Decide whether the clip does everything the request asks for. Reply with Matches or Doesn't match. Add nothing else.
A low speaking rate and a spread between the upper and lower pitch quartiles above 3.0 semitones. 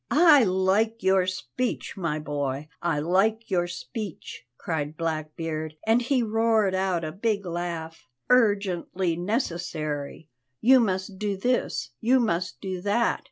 Matches